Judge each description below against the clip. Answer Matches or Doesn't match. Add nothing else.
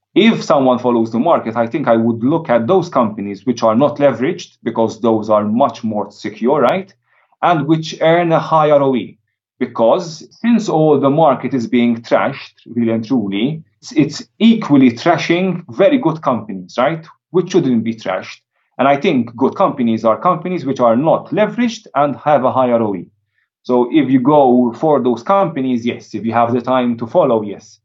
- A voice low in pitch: Matches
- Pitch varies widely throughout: Matches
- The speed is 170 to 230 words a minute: Matches